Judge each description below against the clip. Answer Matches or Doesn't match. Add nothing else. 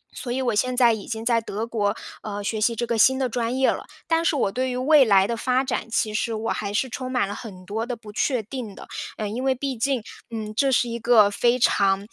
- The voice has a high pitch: Matches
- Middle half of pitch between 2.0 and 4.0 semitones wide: Matches